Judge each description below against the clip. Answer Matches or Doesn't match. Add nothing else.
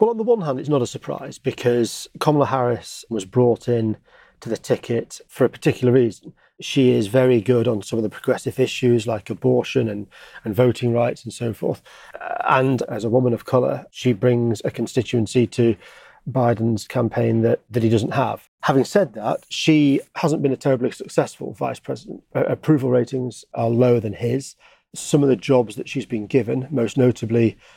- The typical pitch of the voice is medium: Doesn't match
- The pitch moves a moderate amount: Doesn't match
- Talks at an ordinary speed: Matches